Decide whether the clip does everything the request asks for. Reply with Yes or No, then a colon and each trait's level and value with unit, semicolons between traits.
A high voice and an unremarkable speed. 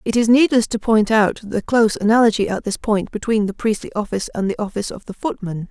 No: high, 215 Hz; fast, 230 wpm